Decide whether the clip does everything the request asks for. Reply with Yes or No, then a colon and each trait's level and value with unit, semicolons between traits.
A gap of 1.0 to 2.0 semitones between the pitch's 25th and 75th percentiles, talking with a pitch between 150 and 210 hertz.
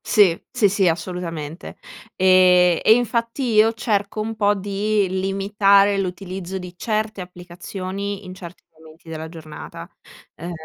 No: narrow, 2.6 semitones; high, 190 Hz